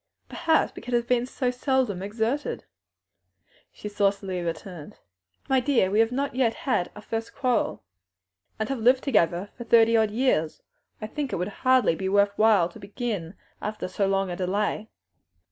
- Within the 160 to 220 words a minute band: Yes, average, 170 wpm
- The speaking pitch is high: Yes, high, 220 Hz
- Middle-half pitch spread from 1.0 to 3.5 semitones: No, average, 4.3 semitones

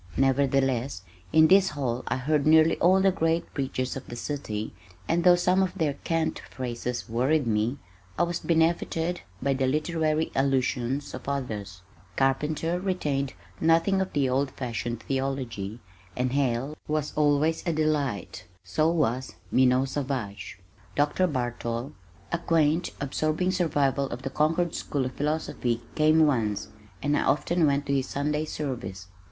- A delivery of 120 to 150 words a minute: Yes, average, 145 wpm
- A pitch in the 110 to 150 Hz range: Yes, medium, 140 Hz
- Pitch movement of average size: Yes, average, 3.8 semitones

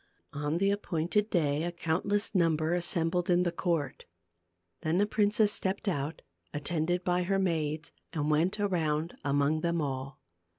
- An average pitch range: Yes, average, 3.3 semitones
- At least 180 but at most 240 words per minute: No, average, 155 wpm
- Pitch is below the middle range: No, medium, 170 Hz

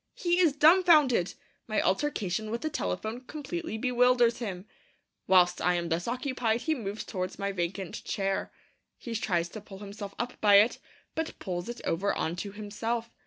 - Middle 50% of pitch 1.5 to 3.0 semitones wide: No, average, 4.6 semitones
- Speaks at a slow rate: No, average, 165 wpm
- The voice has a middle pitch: No, high, 215 Hz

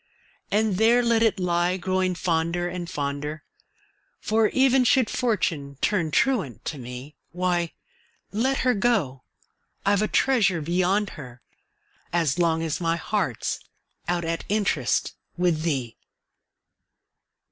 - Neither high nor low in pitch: Yes, medium, 175 Hz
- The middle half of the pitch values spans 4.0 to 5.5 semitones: Yes, average, 5.2 semitones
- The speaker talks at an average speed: No, slow, 125 wpm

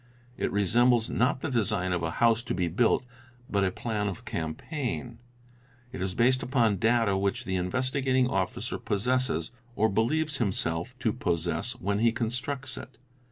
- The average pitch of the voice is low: Yes, low, 115 Hz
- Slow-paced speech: No, average, 160 wpm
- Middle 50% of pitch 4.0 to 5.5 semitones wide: Yes, average, 4.8 semitones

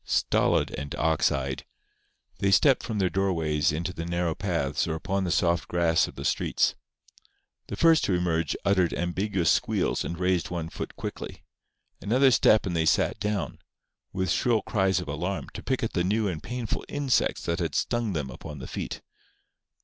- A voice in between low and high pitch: No, very low, 90 Hz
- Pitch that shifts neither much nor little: Yes, average, 3.8 semitones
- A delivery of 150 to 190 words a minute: Yes, average, 180 wpm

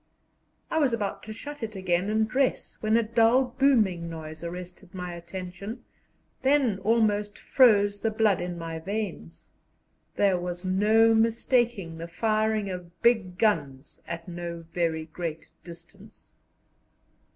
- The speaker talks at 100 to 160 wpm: Yes, slow, 135 wpm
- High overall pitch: Yes, high, 195 Hz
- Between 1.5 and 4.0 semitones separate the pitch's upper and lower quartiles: No, average, 4.4 semitones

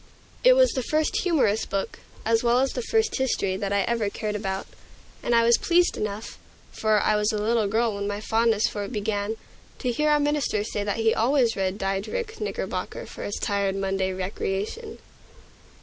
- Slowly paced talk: No, average, 190 wpm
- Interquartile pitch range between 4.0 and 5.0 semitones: Yes, average, 4.3 semitones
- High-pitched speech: Yes, high, 220 Hz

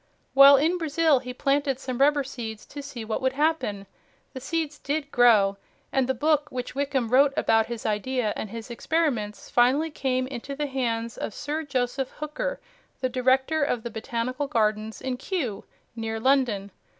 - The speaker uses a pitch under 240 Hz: No, very high, 260 Hz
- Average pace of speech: Yes, average, 170 wpm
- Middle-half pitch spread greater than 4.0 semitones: No, average, 3.7 semitones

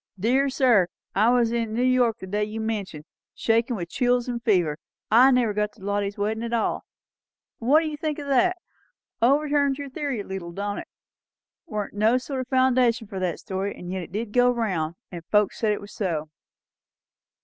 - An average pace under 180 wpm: No, average, 195 wpm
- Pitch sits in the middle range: No, high, 225 Hz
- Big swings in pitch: No, average, 4.0 semitones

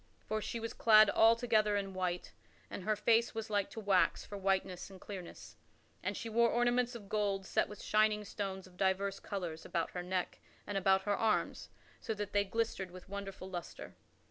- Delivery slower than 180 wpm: No, average, 195 wpm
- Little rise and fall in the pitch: Yes, narrow, 2.2 semitones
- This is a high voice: Yes, high, 200 Hz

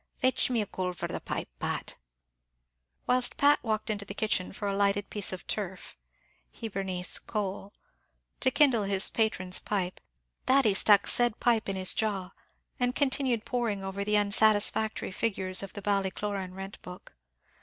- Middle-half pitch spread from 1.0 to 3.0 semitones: Yes, average, 2.7 semitones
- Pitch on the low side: No, high, 205 Hz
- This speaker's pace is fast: No, average, 160 wpm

